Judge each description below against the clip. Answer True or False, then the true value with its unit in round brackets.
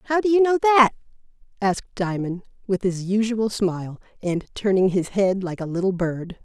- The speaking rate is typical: True (175 wpm)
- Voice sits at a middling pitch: False (205 Hz)